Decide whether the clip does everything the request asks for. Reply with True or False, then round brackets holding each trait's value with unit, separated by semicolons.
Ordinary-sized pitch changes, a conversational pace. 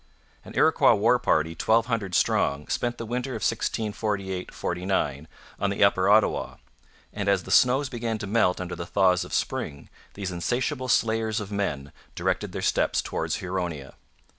True (3.9 semitones; 165 wpm)